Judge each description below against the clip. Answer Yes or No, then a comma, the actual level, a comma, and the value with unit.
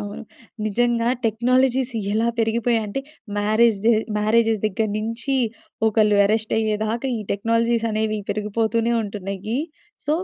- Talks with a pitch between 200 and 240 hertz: Yes, high, 220 Hz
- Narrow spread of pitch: Yes, narrow, 1.6 semitones